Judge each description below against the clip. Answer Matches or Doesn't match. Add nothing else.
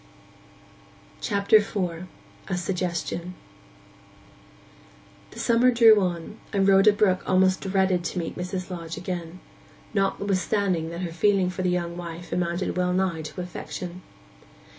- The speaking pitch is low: Doesn't match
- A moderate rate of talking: Doesn't match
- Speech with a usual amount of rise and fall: Doesn't match